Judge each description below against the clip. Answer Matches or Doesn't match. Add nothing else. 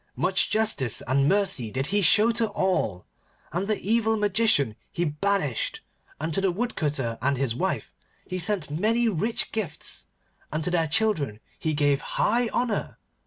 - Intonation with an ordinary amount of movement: Doesn't match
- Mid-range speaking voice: Matches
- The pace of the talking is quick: Doesn't match